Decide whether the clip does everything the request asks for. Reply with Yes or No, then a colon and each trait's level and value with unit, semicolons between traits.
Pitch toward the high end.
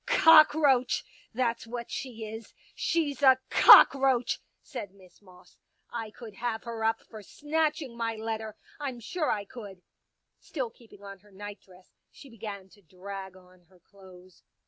Yes: high, 225 Hz